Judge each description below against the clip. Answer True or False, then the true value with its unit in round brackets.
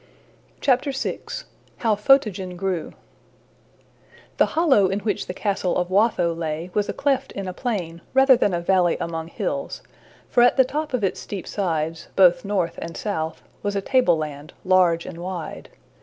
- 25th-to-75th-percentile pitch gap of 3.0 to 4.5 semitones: False (5.0 semitones)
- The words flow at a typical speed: True (160 wpm)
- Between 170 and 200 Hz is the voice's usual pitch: True (190 Hz)